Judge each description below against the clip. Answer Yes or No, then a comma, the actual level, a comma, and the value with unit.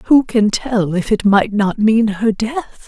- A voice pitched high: Yes, high, 215 Hz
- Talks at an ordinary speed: No, fast, 210 wpm